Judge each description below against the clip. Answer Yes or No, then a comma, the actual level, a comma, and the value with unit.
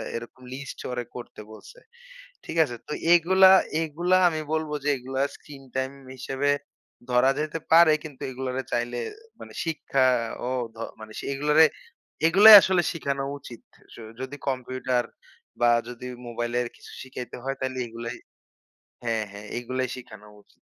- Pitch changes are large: No, average, 4.0 semitones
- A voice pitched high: No, low, 130 Hz